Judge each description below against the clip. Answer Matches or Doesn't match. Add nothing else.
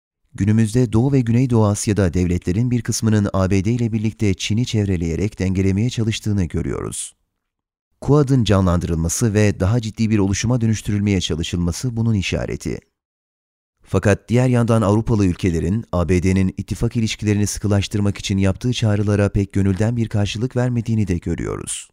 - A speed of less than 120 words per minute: Doesn't match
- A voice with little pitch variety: Doesn't match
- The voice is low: Matches